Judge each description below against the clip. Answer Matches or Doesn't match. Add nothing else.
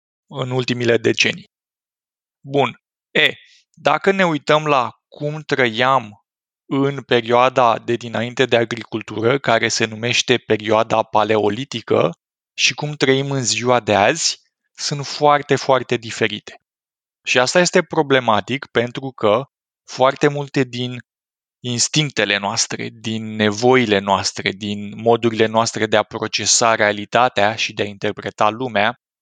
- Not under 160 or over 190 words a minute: Doesn't match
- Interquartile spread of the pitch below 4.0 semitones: Matches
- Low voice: Matches